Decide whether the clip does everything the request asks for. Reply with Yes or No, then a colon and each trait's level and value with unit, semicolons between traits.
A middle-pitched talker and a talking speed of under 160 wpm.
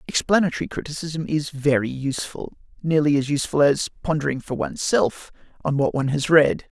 Yes: medium, 145 Hz; average, 150 wpm